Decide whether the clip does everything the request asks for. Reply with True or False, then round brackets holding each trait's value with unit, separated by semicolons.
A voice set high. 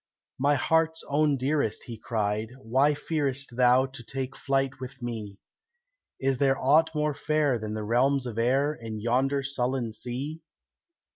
False (135 Hz)